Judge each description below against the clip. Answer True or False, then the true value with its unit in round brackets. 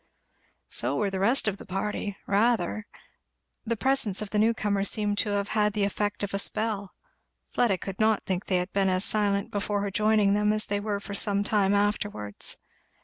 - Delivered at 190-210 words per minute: True (195 wpm)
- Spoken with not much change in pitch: True (1.2 semitones)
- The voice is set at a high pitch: True (205 Hz)